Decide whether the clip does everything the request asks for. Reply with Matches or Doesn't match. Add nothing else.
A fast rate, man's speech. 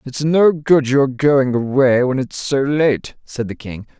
Doesn't match